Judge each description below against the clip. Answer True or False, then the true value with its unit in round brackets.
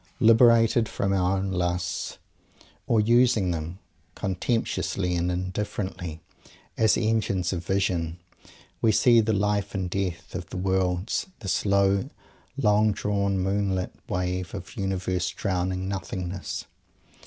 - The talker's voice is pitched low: True (95 Hz)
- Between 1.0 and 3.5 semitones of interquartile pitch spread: True (2.5 semitones)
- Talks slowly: True (120 wpm)